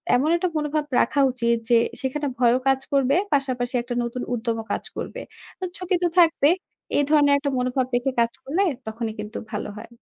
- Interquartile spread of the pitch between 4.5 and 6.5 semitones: No, average, 3.7 semitones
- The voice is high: Yes, very high, 260 Hz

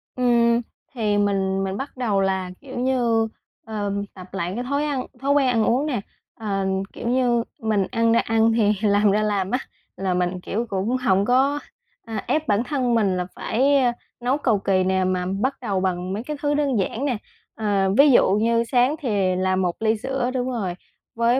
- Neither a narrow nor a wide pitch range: Yes, average, 4.4 semitones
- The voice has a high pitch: Yes, high, 225 Hz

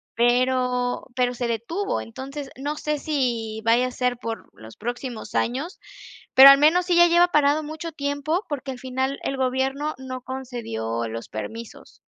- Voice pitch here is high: Yes, very high, 260 Hz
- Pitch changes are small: No, average, 3.3 semitones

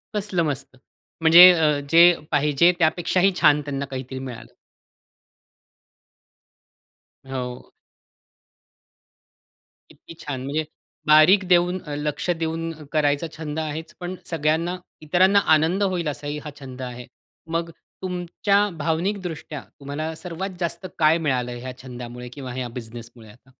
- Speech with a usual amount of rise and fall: Yes, average, 4.2 semitones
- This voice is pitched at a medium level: Yes, medium, 155 Hz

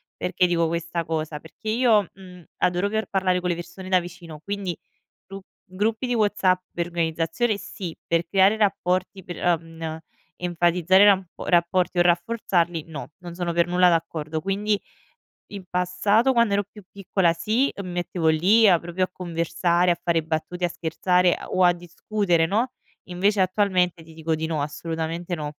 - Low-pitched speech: No, medium, 180 Hz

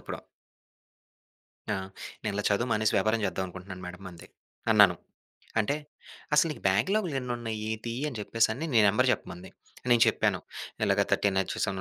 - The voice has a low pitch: Yes, low, 110 Hz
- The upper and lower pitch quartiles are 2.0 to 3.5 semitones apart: No, average, 4.0 semitones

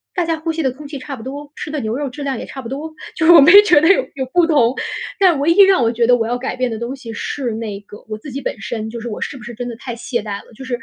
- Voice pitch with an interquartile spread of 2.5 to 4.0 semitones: No, average, 4.4 semitones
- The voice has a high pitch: Yes, very high, 265 Hz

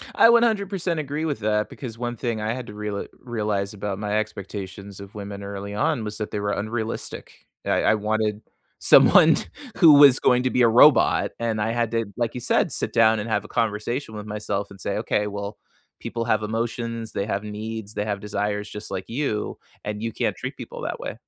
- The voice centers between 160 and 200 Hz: No, low, 110 Hz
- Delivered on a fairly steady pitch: Yes, narrow, 2.3 semitones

